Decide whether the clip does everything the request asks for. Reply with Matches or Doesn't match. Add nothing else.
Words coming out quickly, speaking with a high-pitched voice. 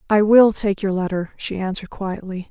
Doesn't match